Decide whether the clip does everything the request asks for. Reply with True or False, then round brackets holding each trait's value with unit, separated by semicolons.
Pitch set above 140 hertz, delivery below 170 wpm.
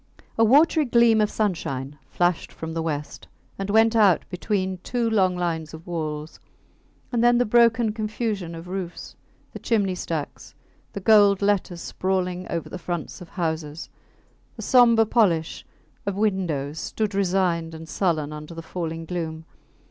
True (185 Hz; 150 wpm)